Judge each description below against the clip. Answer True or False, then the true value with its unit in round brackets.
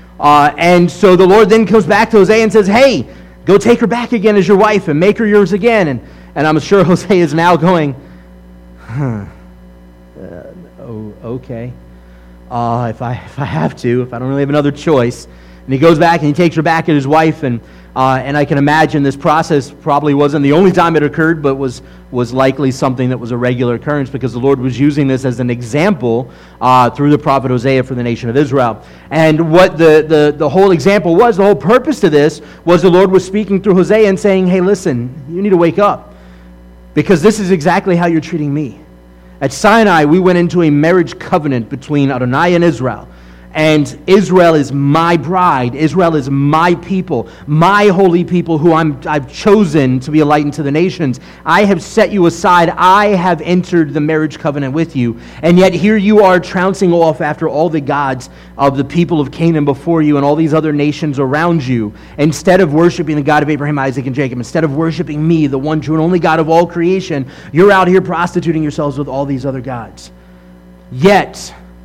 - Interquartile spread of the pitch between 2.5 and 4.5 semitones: False (5.3 semitones)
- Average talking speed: False (210 wpm)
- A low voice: False (150 Hz)